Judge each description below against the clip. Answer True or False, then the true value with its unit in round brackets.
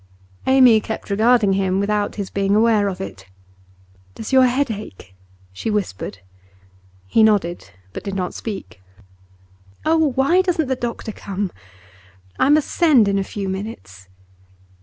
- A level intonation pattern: False (4.4 semitones)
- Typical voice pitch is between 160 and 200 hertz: False (210 Hz)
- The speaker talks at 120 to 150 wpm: True (140 wpm)